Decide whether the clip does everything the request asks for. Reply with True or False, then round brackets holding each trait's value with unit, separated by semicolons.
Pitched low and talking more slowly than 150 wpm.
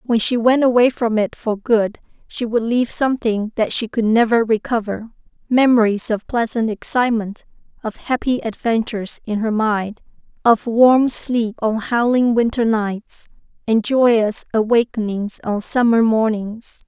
False (225 Hz; 140 wpm)